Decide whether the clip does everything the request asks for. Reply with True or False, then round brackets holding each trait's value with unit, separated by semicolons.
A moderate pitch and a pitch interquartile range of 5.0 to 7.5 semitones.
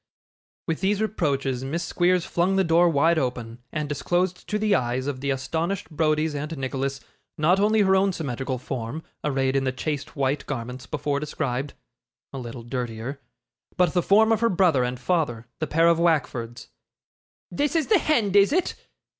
True (150 Hz; 5.4 semitones)